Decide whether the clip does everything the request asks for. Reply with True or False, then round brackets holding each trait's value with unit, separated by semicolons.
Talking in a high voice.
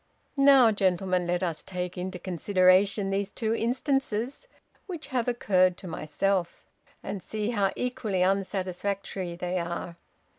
True (195 Hz)